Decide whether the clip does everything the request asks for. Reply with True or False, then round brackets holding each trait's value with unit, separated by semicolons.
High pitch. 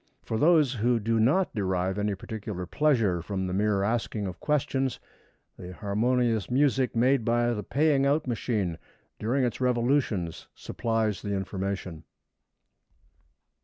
False (115 Hz)